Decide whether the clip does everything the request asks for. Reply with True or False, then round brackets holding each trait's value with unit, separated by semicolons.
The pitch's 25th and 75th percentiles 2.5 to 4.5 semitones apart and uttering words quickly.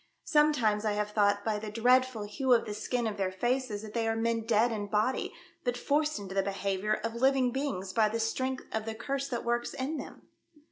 True (3.5 semitones; 220 wpm)